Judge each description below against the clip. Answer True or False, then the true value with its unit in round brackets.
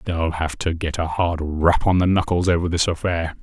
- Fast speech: True (225 wpm)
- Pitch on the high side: False (85 Hz)